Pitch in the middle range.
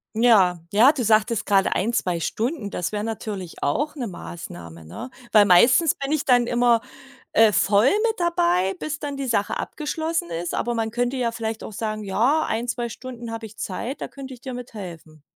No: high, 225 Hz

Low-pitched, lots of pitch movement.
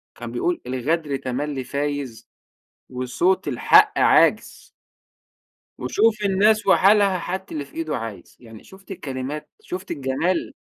No: medium, 155 Hz; wide, 6.5 semitones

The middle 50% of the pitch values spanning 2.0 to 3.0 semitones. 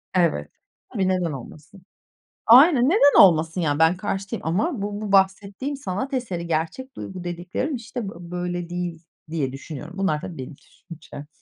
No: average, 4.3 semitones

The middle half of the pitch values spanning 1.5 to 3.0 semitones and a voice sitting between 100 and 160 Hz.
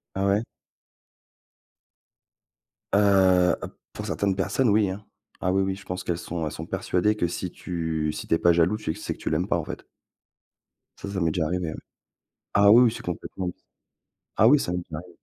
No: average, 2.7 semitones; very low, 90 Hz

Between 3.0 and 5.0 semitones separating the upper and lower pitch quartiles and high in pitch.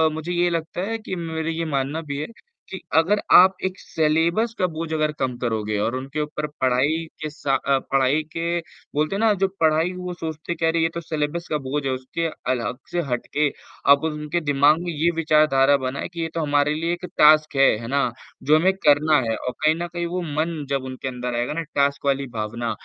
No: average, 3.5 semitones; medium, 155 Hz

